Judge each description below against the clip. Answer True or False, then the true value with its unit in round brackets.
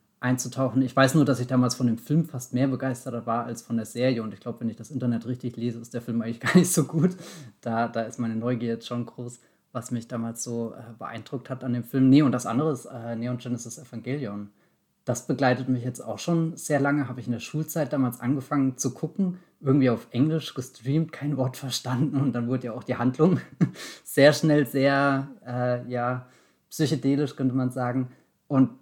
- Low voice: True (125 Hz)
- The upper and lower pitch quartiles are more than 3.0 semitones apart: False (2.6 semitones)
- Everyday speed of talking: False (215 wpm)